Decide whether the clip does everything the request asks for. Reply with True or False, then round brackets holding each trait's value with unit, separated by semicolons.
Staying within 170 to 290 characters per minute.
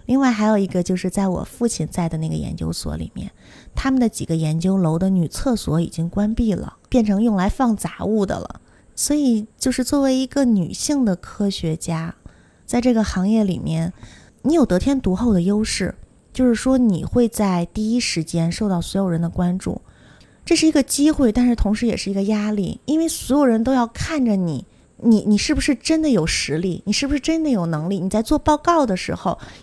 False (300 characters per minute)